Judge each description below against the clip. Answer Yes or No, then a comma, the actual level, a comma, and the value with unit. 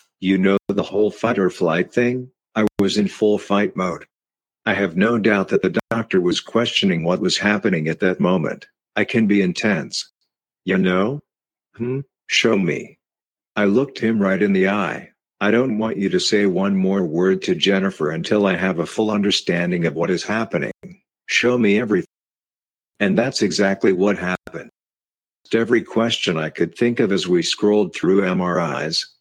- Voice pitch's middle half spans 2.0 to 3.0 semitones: Yes, average, 2.7 semitones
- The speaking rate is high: No, average, 175 wpm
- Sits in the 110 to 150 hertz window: No, low, 100 Hz